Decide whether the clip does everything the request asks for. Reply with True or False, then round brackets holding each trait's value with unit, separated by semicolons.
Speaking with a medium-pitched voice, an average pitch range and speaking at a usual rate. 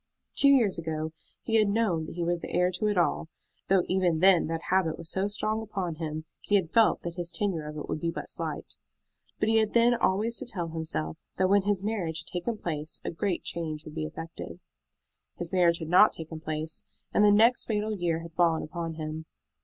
False (175 Hz; 4.2 semitones; 220 wpm)